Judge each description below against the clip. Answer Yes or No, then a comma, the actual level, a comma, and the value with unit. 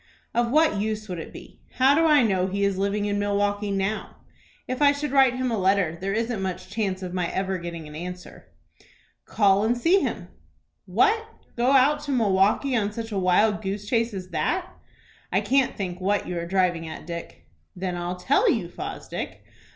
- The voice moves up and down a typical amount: Yes, average, 4.6 semitones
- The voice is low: No, high, 205 Hz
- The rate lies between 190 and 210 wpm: Yes, average, 195 wpm